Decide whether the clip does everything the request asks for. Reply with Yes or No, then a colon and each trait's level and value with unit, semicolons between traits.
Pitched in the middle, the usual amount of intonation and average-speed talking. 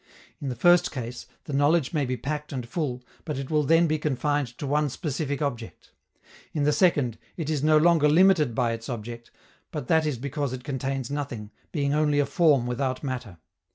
Yes: medium, 145 Hz; average, 3.2 semitones; average, 195 wpm